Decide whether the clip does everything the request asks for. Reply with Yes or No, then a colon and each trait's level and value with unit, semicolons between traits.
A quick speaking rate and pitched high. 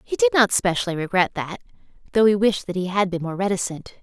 Yes: fast, 225 wpm; high, 195 Hz